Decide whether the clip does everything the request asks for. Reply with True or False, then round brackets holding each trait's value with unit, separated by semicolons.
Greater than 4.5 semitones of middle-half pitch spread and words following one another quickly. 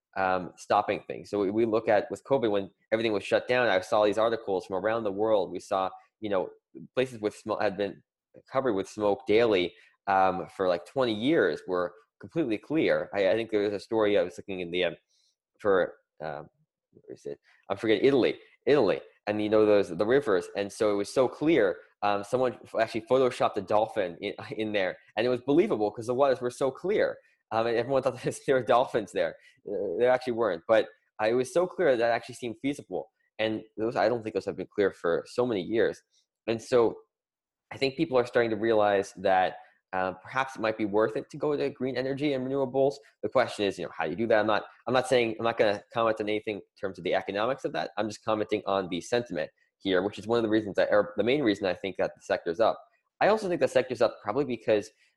True (5.3 semitones; 235 wpm)